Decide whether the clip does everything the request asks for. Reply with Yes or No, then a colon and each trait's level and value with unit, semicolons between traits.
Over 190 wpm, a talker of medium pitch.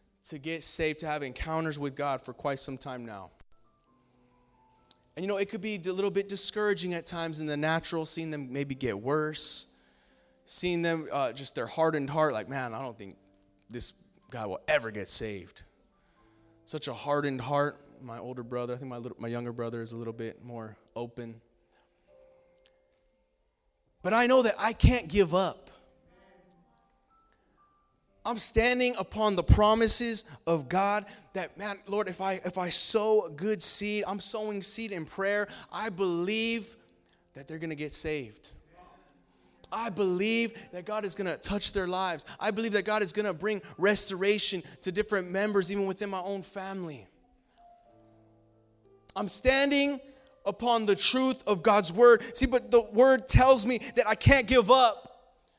No: average, 170 wpm; medium, 170 Hz